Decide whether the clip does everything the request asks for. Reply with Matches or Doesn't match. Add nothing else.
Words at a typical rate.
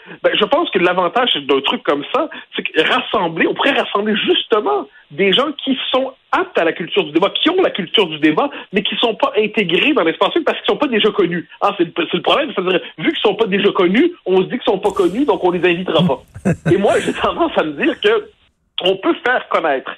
Doesn't match